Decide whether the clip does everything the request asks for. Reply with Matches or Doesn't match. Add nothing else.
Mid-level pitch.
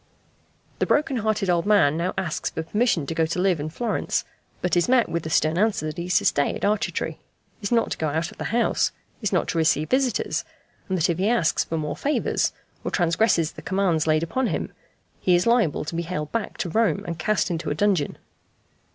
Matches